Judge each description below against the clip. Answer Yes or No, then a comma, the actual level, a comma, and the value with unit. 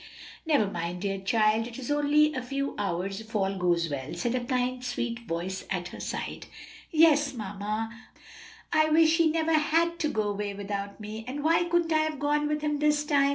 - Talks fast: Yes, fast, 210 wpm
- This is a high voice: Yes, high, 245 Hz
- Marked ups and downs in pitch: Yes, wide, 7.0 semitones